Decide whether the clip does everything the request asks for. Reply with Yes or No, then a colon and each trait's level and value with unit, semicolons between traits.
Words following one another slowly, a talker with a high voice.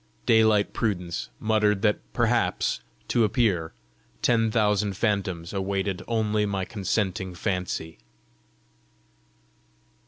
No: slow, 90 wpm; low, 100 Hz